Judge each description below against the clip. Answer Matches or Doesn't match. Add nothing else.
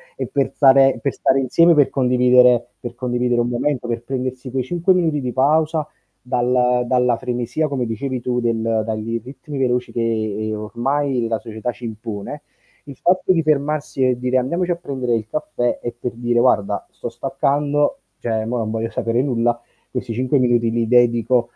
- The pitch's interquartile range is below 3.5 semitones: Matches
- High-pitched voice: Doesn't match